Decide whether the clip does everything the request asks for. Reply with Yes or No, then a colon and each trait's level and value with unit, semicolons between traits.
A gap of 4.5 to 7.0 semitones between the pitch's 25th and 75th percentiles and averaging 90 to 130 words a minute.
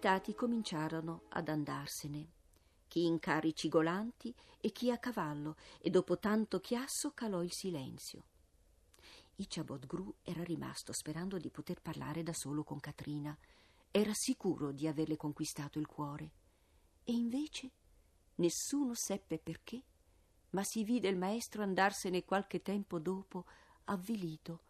Yes: average, 5.0 semitones; average, 125 wpm